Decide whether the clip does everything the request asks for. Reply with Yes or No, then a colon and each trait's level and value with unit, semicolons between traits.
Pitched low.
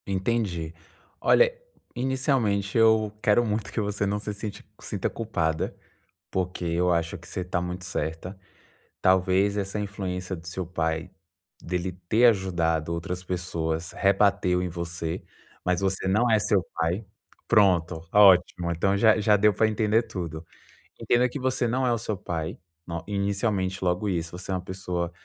Yes: very low, 95 Hz